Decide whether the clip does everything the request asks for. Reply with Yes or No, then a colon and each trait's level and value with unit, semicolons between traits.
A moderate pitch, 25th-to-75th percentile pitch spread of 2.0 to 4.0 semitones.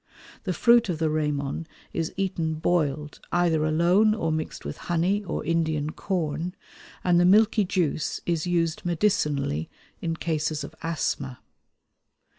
Yes: medium, 165 Hz; narrow, 2.6 semitones